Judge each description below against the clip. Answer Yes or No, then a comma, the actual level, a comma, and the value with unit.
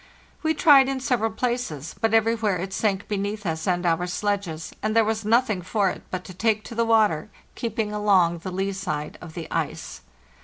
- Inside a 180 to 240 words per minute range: Yes, average, 200 wpm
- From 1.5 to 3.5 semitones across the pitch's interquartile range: No, average, 3.9 semitones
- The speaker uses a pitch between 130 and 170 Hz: No, high, 205 Hz